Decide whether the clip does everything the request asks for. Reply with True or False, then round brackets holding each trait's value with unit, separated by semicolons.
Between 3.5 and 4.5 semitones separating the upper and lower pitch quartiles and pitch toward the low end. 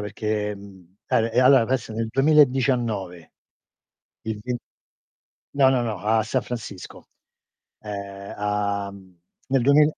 True (4.0 semitones; 110 Hz)